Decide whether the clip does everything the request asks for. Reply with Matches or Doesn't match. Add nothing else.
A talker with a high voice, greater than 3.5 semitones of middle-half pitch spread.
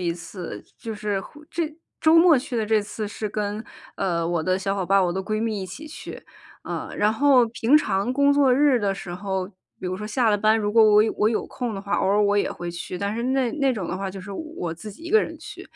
Matches